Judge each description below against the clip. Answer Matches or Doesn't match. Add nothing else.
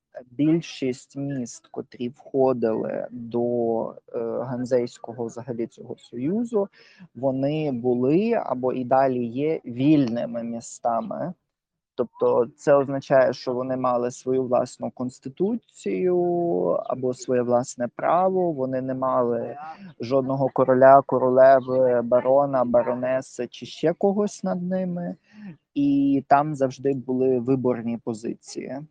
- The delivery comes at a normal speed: Doesn't match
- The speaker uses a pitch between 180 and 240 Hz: Doesn't match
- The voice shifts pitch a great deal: Doesn't match